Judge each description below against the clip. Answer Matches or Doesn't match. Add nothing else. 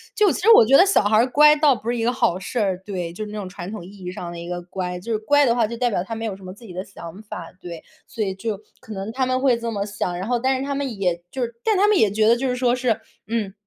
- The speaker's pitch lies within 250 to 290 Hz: Doesn't match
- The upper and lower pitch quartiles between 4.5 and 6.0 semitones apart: Matches